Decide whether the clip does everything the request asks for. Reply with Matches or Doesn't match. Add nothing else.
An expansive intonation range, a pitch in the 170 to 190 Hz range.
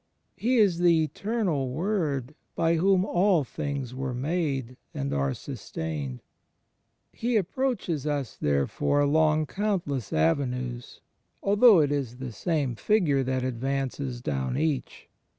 Doesn't match